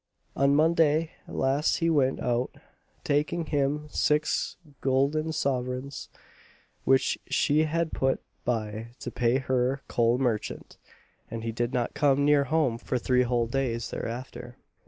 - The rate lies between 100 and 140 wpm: Yes, slow, 135 wpm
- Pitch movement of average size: Yes, average, 3.3 semitones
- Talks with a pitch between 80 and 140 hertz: Yes, low, 135 Hz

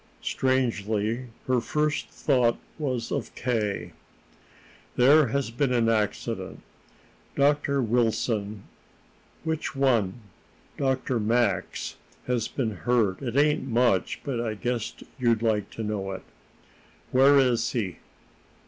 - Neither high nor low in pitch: No, low, 120 Hz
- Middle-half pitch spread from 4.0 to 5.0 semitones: No, average, 3.4 semitones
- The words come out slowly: Yes, slow, 115 wpm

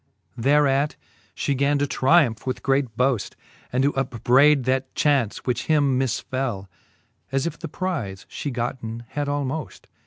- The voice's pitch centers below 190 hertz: Yes, low, 135 Hz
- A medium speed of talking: Yes, average, 150 wpm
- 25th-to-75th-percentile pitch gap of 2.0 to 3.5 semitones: Yes, average, 2.7 semitones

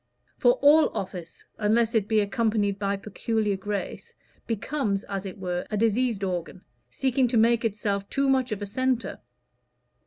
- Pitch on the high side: Yes, high, 215 Hz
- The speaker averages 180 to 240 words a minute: No, average, 155 wpm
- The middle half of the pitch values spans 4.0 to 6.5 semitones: No, average, 3.1 semitones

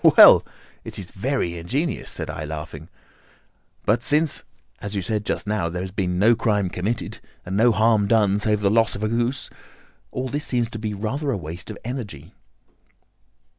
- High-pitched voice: No, low, 105 Hz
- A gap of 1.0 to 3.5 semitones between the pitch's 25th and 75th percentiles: No, average, 3.9 semitones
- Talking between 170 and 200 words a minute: Yes, average, 180 wpm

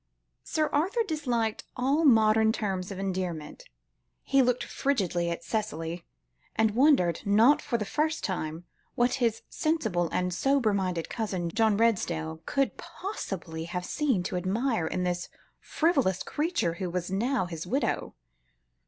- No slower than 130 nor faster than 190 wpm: Yes, average, 140 wpm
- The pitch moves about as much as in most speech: No, wide, 6.8 semitones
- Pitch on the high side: Yes, high, 210 Hz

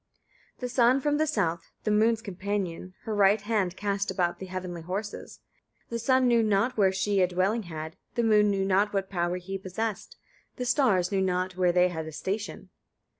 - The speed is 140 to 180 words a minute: No, average, 195 wpm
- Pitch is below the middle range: No, high, 195 Hz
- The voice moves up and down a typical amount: Yes, average, 3.3 semitones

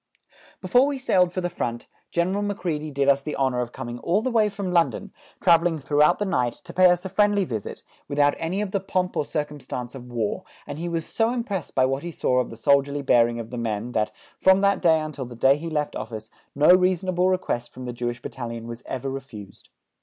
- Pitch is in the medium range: Yes, medium, 150 Hz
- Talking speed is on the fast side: Yes, fast, 220 wpm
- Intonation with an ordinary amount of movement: No, wide, 6.9 semitones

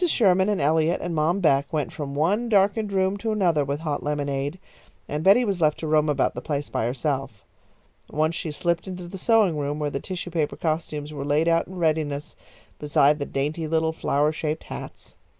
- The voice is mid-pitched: Yes, medium, 155 Hz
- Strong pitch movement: No, average, 3.6 semitones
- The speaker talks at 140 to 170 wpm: No, average, 200 wpm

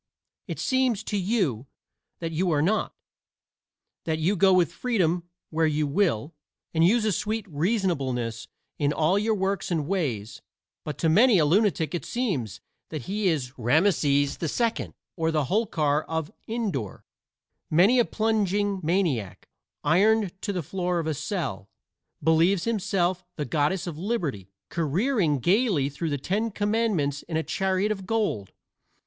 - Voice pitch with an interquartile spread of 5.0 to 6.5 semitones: Yes, wide, 5.5 semitones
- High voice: No, medium, 175 Hz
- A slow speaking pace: No, average, 150 wpm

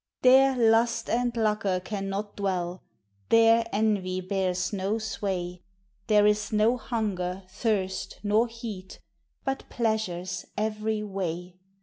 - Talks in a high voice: Yes, high, 210 Hz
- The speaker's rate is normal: No, slow, 110 wpm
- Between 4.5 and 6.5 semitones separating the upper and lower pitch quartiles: No, average, 3.2 semitones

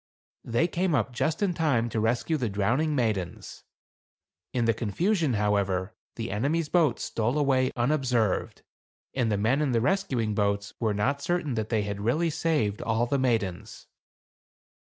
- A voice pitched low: Yes, low, 120 Hz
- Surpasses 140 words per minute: Yes, average, 155 wpm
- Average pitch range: No, wide, 5.7 semitones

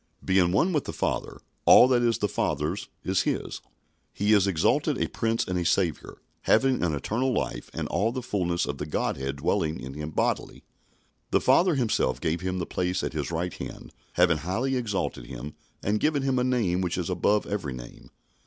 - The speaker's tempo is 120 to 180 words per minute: No, average, 195 wpm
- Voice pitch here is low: Yes, very low, 95 Hz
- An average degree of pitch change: No, wide, 6.4 semitones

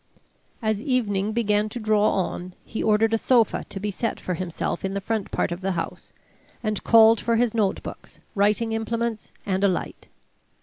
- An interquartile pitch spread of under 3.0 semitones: Yes, narrow, 2.5 semitones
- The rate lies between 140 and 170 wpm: No, average, 180 wpm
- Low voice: No, high, 215 Hz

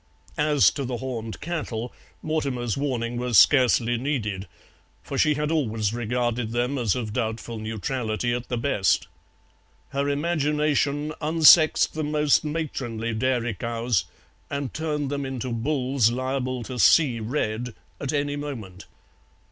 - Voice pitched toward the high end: No, low, 125 Hz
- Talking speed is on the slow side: Yes, slow, 130 wpm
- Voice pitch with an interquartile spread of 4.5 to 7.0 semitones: No, average, 3.9 semitones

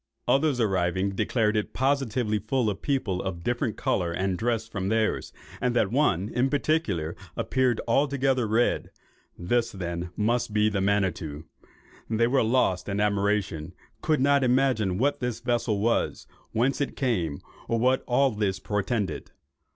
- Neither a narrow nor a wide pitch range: Yes, average, 4.7 semitones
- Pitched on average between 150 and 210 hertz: No, low, 110 Hz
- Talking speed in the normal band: Yes, average, 155 wpm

